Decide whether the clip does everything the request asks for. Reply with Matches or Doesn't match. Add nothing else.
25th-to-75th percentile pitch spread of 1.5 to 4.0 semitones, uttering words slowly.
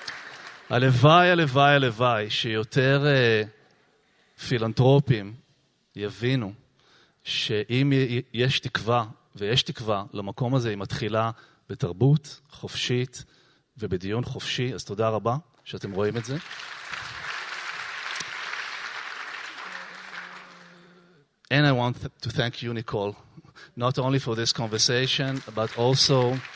Matches